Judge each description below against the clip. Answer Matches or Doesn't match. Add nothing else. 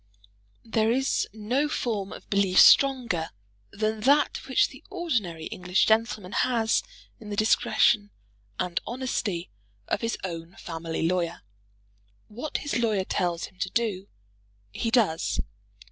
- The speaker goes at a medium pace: Doesn't match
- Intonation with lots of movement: Doesn't match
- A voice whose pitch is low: Doesn't match